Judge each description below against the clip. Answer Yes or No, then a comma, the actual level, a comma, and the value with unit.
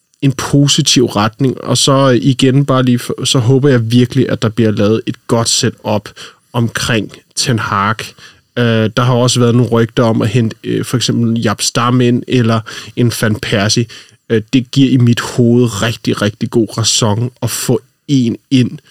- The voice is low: Yes, low, 120 Hz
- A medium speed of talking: Yes, average, 170 wpm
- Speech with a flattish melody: Yes, narrow, 2.3 semitones